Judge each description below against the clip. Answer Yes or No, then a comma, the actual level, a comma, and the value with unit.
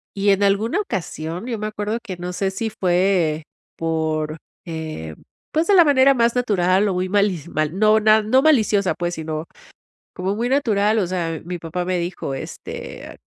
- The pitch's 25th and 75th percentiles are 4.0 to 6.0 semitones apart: Yes, average, 4.4 semitones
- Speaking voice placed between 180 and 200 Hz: Yes, high, 190 Hz